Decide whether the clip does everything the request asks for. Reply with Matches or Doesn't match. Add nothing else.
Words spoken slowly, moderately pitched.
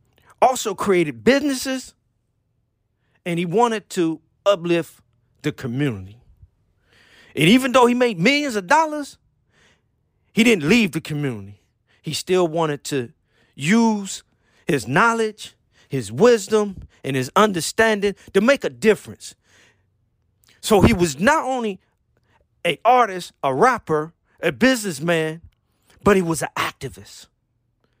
Matches